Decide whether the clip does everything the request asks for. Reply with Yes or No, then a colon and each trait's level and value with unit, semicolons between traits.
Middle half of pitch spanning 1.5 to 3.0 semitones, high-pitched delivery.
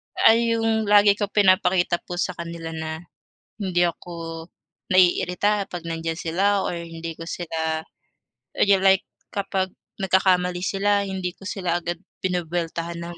No: narrow, 2.6 semitones; medium, 180 Hz